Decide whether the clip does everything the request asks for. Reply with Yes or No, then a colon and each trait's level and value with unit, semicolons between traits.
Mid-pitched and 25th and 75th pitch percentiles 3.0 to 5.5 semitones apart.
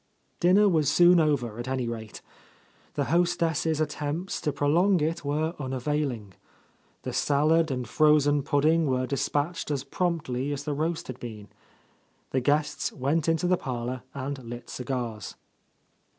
Yes: medium, 145 Hz; average, 3.9 semitones